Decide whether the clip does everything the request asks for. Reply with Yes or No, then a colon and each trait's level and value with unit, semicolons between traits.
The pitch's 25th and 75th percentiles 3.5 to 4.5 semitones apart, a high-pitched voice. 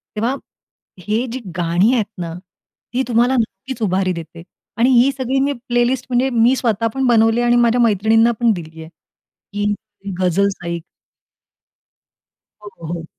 Yes: average, 4.2 semitones; high, 225 Hz